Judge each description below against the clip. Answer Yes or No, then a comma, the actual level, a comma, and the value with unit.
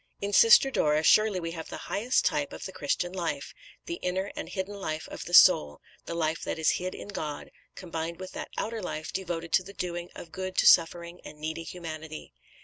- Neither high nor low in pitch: Yes, medium, 175 Hz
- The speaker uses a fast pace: Yes, fast, 210 wpm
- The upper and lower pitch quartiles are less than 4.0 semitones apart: Yes, average, 2.9 semitones